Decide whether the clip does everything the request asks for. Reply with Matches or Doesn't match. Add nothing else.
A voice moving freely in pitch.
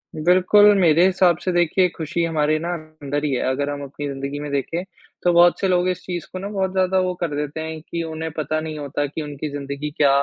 Doesn't match